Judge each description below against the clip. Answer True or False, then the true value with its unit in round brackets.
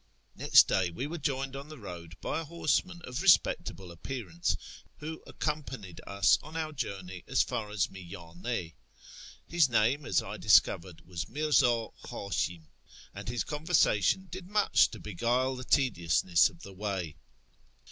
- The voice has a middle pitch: False (115 Hz)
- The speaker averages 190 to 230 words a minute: False (145 wpm)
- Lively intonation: True (8.5 semitones)